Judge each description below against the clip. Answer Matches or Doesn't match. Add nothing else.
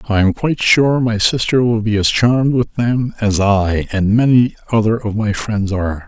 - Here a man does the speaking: Matches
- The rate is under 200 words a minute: Doesn't match